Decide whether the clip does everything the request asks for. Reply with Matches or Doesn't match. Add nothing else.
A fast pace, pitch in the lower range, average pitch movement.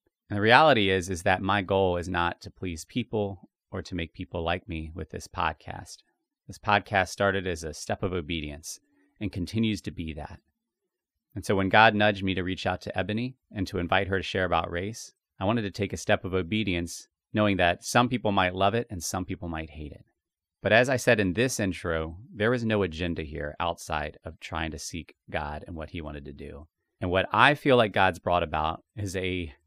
Matches